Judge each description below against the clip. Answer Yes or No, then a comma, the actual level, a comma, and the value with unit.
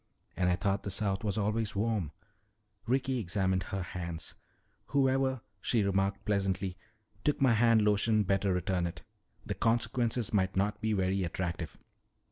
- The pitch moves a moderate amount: Yes, average, 3.3 semitones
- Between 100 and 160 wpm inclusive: Yes, average, 145 wpm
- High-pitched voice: No, low, 100 Hz